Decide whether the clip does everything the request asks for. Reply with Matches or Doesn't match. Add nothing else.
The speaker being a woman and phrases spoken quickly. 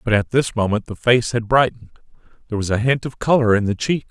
Doesn't match